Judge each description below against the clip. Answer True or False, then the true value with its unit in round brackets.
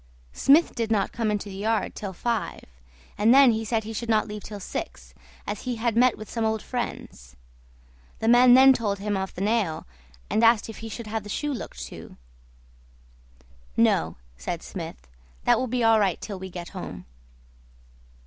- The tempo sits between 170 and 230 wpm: True (185 wpm)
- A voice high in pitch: True (220 Hz)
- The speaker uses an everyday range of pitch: True (3.0 semitones)